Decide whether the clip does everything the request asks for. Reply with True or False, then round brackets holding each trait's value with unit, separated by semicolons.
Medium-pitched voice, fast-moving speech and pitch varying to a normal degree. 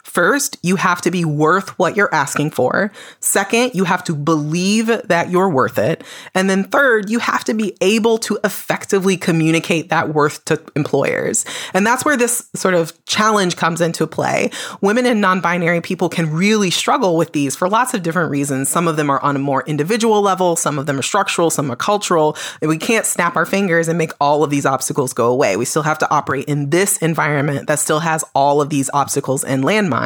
True (170 Hz; 210 wpm; 4.9 semitones)